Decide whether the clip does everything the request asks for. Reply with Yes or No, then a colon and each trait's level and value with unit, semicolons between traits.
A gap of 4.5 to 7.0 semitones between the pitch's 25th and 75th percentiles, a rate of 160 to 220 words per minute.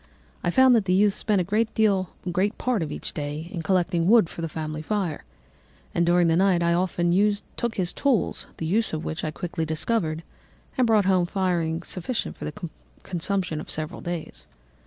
No: average, 3.7 semitones; average, 185 wpm